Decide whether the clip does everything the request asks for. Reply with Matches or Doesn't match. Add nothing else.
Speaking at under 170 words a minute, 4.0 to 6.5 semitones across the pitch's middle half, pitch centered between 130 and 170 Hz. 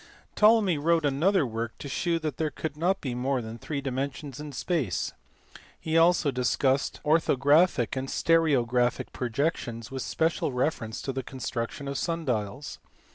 Matches